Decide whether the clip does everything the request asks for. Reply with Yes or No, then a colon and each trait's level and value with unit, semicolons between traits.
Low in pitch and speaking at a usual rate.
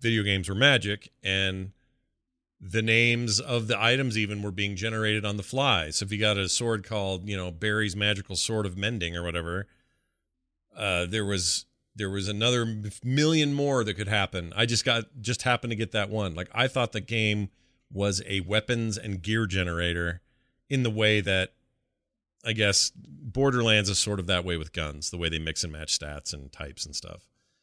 Yes: low, 105 Hz; average, 195 wpm